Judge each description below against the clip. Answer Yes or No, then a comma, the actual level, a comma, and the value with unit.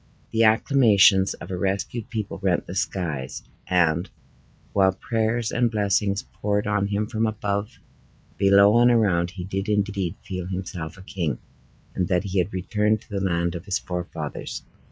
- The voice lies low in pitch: Yes, low, 100 Hz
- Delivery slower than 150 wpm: No, average, 160 wpm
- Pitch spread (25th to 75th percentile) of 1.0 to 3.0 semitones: Yes, narrow, 2.6 semitones